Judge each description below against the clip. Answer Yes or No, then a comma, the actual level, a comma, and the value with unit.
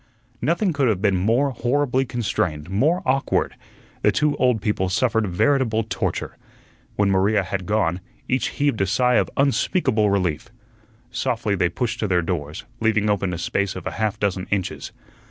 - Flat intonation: No, average, 5.1 semitones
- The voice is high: No, low, 105 Hz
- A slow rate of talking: No, average, 165 wpm